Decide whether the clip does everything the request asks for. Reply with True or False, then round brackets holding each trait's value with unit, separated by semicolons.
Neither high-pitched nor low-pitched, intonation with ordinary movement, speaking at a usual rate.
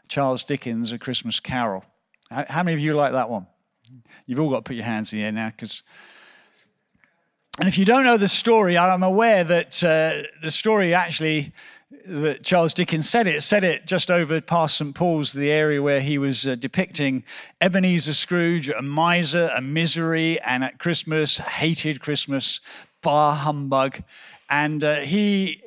True (155 Hz; 4.2 semitones; 170 wpm)